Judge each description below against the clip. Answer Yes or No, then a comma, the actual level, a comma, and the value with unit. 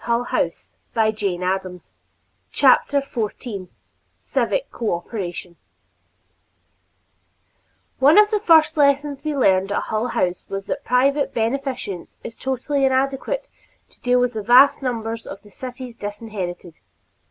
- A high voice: Yes, high, 245 Hz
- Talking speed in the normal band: No, slow, 120 wpm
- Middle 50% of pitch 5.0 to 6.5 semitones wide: Yes, average, 5.3 semitones